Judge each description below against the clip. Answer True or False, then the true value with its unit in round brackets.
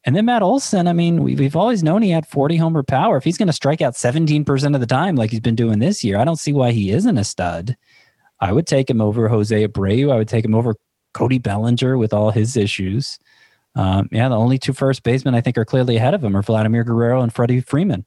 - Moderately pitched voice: False (125 Hz)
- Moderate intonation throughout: True (4.6 semitones)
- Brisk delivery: True (250 wpm)